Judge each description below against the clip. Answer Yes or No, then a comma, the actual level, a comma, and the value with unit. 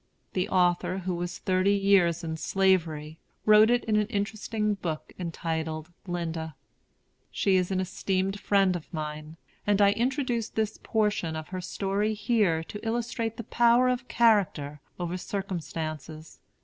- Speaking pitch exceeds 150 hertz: Yes, high, 190 Hz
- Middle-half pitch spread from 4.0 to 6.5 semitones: Yes, average, 4.3 semitones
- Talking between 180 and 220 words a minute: No, average, 145 wpm